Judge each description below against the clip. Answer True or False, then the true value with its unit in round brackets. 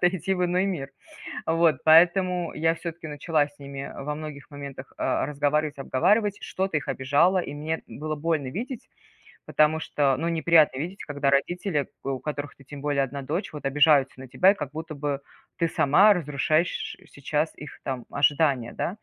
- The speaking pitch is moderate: True (150 Hz)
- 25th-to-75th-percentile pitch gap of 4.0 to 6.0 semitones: False (3.1 semitones)